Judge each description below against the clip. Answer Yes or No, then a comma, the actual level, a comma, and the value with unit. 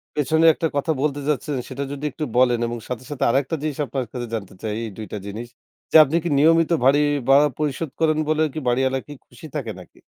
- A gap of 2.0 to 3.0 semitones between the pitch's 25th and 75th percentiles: No, average, 3.6 semitones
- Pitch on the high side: No, medium, 140 Hz